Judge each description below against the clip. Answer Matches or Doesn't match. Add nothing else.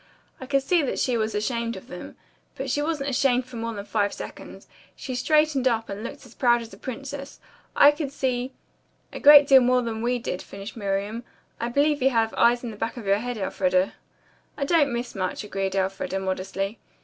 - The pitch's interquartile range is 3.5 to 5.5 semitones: Matches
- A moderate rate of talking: Doesn't match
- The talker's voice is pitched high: Matches